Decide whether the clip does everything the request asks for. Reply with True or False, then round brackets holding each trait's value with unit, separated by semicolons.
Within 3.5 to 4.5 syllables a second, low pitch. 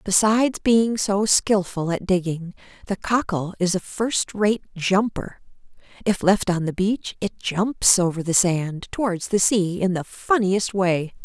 False (4.0 syllables/s; 195 Hz)